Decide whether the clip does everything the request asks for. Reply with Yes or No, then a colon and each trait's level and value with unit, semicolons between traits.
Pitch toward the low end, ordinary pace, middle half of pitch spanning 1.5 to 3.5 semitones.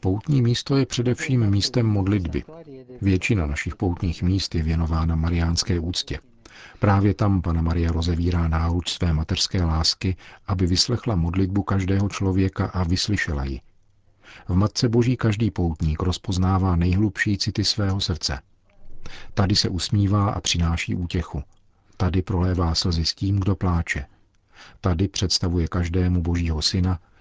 Yes: very low, 95 Hz; average, 130 wpm; average, 2.8 semitones